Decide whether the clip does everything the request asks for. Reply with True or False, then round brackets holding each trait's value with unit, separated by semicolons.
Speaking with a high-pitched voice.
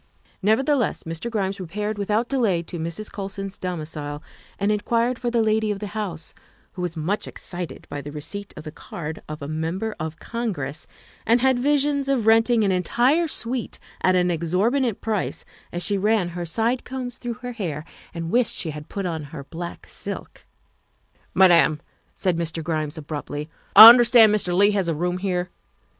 True (195 Hz)